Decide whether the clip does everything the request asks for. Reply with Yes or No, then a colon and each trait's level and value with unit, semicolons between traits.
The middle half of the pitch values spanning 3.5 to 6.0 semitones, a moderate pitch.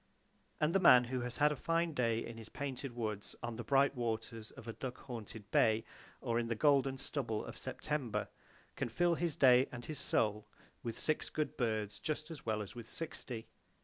No: average, 4.0 semitones; low, 125 Hz